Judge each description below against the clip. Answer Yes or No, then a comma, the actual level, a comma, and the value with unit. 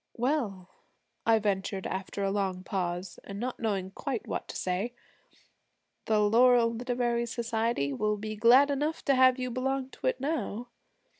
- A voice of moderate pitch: No, high, 230 Hz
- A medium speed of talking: Yes, average, 155 wpm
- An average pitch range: Yes, average, 4.2 semitones